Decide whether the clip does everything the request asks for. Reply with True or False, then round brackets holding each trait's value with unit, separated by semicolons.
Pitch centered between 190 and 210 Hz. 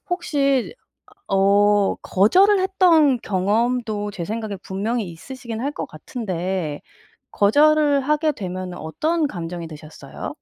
False (220 Hz)